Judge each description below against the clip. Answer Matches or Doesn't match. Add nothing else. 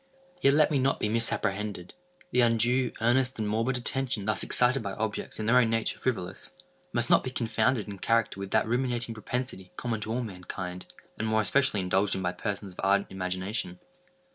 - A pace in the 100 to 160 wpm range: Doesn't match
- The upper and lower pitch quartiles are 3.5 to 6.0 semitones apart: Matches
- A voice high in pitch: Doesn't match